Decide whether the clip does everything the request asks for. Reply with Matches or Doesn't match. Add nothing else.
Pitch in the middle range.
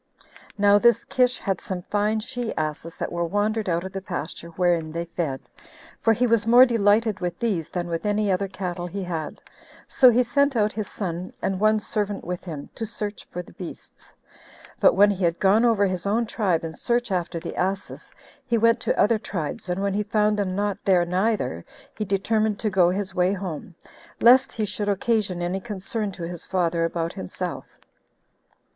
Doesn't match